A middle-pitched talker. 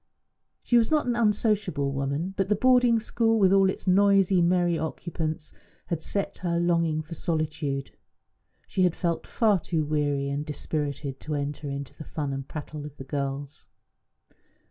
Yes: medium, 165 Hz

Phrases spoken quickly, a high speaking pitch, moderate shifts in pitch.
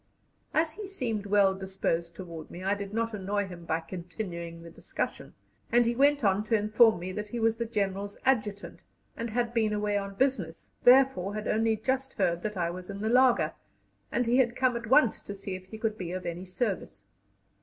Yes: fast, 210 wpm; high, 210 Hz; average, 4.0 semitones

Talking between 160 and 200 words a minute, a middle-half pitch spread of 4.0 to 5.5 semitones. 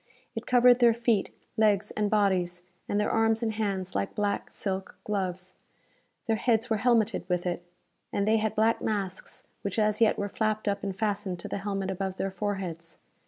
No: average, 185 wpm; narrow, 2.5 semitones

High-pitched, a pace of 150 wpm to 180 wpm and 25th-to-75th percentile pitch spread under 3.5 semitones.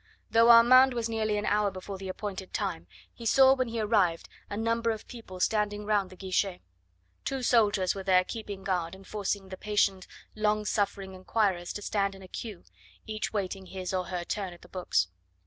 No: high, 205 Hz; average, 195 wpm; average, 2.7 semitones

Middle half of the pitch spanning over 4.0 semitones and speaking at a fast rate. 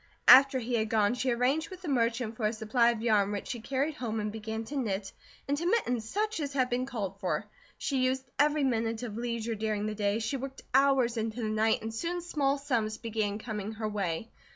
No: average, 3.7 semitones; fast, 220 wpm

